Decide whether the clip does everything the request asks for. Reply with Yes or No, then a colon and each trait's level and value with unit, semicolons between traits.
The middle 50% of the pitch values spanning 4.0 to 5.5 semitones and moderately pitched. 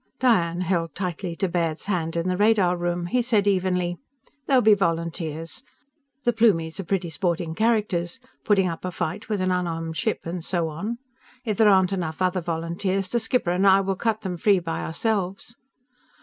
No: average, 3.3 semitones; medium, 180 Hz